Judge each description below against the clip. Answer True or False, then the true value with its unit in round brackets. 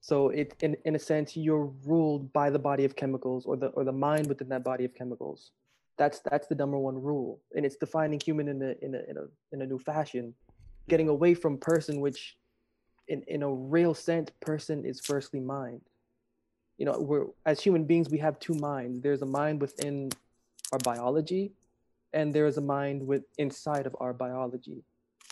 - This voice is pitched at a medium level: True (145 Hz)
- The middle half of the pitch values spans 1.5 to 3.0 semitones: True (2.6 semitones)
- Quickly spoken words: False (195 wpm)